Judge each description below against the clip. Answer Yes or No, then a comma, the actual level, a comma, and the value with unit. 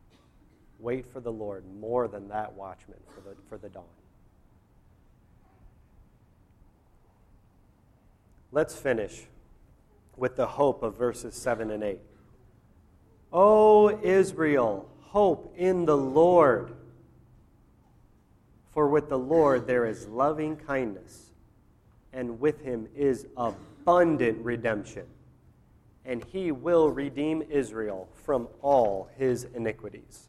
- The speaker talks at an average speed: No, slow, 105 wpm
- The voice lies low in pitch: Yes, low, 120 Hz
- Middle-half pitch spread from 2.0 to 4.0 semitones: No, average, 5.3 semitones